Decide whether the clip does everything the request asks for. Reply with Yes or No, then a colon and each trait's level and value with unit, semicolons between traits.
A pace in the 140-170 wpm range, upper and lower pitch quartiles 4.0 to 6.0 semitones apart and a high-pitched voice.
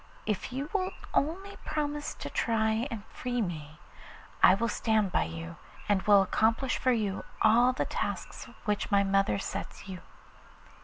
Yes: average, 155 wpm; average, 4.5 semitones; high, 220 Hz